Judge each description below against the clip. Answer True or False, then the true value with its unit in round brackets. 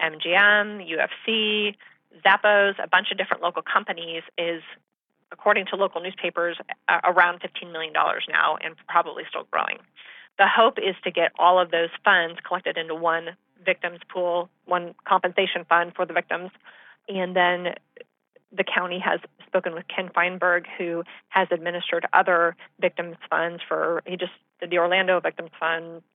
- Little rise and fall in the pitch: True (2.0 semitones)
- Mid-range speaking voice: True (180 Hz)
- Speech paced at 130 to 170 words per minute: True (150 wpm)